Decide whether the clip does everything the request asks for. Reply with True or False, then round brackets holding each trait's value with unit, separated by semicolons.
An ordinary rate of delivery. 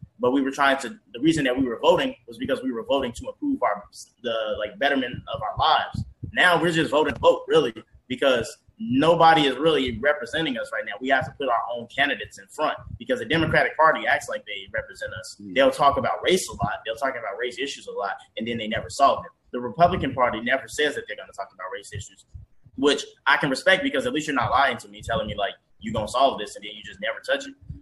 False (250 wpm)